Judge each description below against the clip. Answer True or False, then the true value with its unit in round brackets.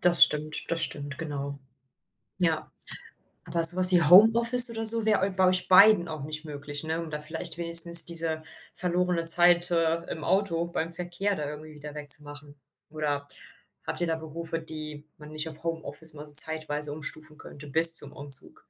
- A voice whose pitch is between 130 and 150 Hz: False (160 Hz)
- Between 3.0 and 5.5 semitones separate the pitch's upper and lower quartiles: False (2.5 semitones)